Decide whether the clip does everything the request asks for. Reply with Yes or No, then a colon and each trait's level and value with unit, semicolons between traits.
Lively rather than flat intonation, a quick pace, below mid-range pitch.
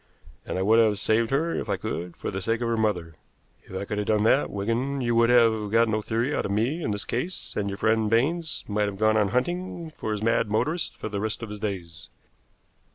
No: narrow, 2.5 semitones; fast, 245 wpm; low, 110 Hz